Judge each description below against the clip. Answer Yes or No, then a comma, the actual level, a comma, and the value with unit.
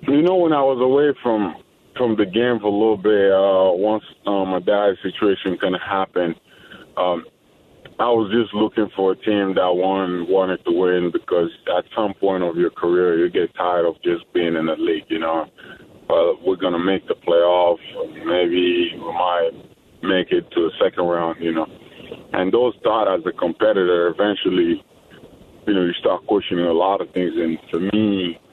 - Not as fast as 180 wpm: No, average, 190 wpm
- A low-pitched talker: Yes, low, 110 Hz